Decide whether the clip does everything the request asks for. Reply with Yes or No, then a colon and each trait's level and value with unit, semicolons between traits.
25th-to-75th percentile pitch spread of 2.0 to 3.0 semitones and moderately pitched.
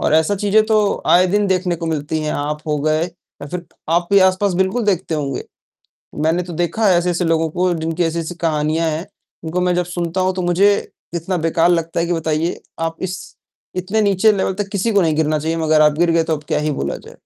Yes: narrow, 2.6 semitones; medium, 170 Hz